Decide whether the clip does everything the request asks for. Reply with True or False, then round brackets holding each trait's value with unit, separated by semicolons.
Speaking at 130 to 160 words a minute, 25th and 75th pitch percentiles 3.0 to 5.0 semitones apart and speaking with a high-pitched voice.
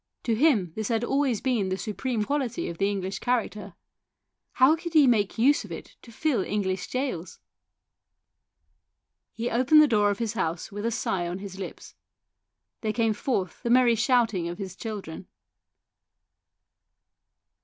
True (155 wpm; 4.3 semitones; 220 Hz)